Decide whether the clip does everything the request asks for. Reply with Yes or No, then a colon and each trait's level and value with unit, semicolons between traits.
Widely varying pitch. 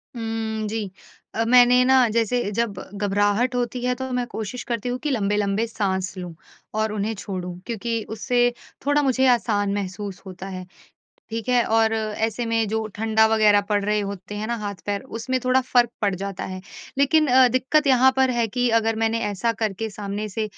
No: average, 3.1 semitones